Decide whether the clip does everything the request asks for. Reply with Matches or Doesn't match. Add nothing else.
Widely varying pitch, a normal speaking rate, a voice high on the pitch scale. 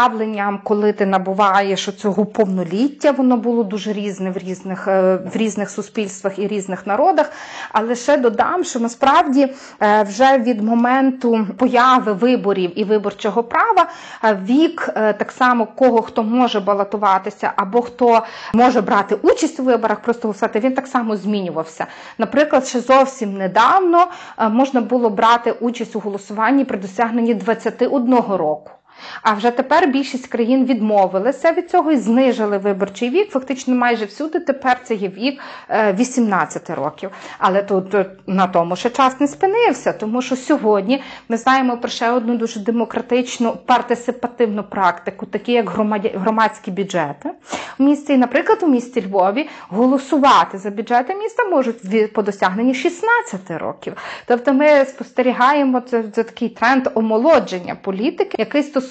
Doesn't match